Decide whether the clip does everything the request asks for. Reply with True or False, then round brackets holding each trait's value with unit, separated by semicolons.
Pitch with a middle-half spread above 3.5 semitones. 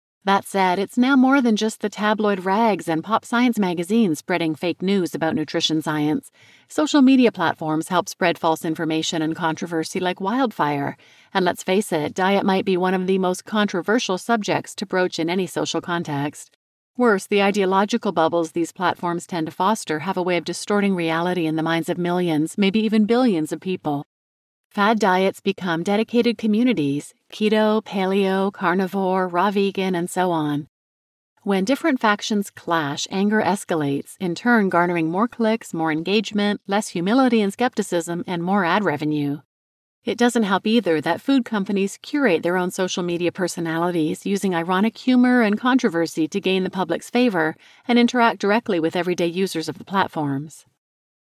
True (4.4 semitones)